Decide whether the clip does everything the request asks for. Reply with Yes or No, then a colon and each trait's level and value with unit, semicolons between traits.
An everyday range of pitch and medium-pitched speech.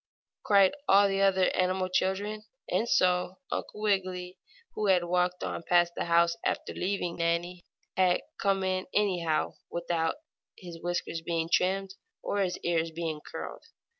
No: narrow, 2.0 semitones; medium, 180 Hz